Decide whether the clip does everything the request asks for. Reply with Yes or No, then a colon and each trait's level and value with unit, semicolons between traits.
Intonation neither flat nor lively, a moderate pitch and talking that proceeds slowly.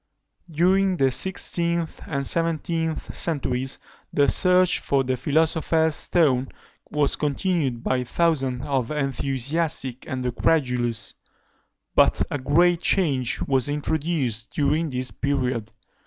Yes: average, 4.2 semitones; medium, 145 Hz; slow, 115 wpm